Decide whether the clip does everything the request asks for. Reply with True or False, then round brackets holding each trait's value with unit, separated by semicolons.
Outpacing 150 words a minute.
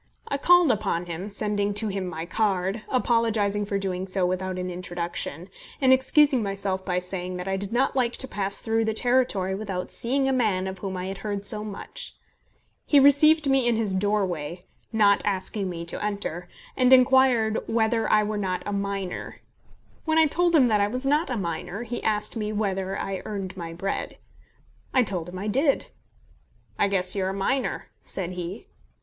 True (190 wpm)